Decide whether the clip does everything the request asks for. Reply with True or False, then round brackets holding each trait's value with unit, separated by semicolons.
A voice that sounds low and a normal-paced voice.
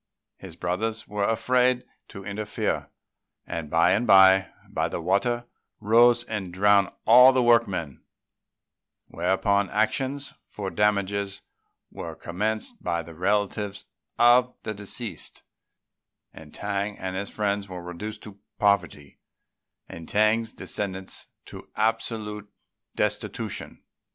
False (100 Hz; 110 wpm)